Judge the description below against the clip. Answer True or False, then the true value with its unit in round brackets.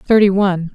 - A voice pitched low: False (195 Hz)